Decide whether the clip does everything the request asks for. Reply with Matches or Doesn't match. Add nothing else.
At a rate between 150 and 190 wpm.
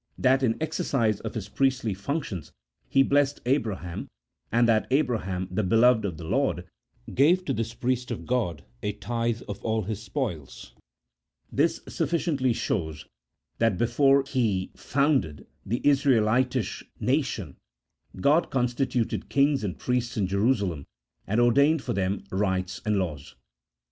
Doesn't match